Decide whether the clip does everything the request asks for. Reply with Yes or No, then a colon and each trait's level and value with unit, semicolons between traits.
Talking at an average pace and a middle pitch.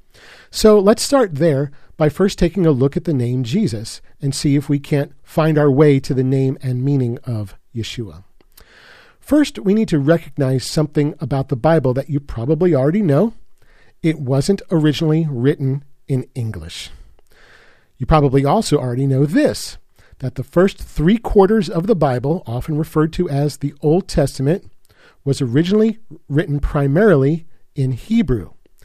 Yes: average, 155 wpm; medium, 150 Hz